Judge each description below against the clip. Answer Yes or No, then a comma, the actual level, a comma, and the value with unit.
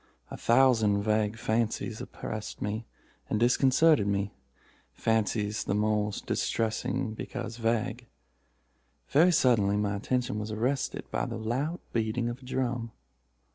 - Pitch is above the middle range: No, low, 110 Hz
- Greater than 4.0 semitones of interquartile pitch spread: No, average, 2.7 semitones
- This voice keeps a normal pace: No, slow, 115 wpm